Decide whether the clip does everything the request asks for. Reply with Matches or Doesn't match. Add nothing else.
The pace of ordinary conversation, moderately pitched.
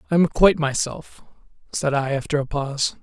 Matches